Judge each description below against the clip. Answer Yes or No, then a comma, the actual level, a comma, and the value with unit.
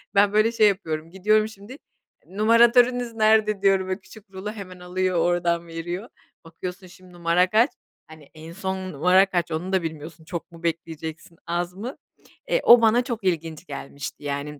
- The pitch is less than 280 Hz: Yes, medium, 185 Hz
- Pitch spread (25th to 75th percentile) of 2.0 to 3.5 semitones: No, average, 4.2 semitones